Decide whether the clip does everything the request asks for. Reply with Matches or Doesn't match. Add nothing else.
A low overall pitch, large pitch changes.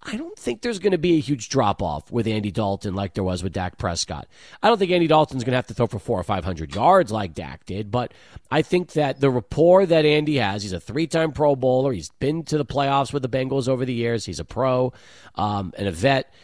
Matches